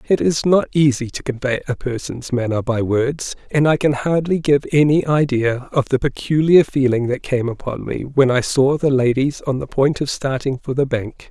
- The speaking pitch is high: No, low, 135 Hz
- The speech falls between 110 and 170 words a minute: No, fast, 205 wpm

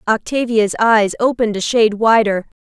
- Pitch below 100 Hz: No, high, 220 Hz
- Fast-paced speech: No, slow, 135 wpm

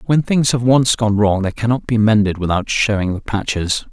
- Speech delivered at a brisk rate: Yes, fast, 215 wpm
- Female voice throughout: No, male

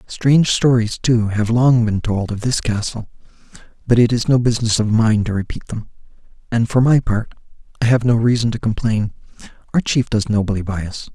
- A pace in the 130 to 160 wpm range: No, average, 195 wpm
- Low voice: Yes, low, 115 Hz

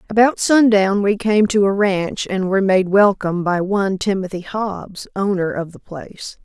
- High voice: Yes, high, 195 Hz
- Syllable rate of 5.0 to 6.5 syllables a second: No, 4.7 syllables/s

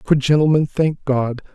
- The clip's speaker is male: Yes, male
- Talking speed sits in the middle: Yes, average, 155 wpm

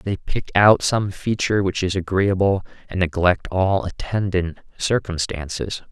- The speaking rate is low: Yes, slow, 130 wpm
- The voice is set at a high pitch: No, very low, 95 Hz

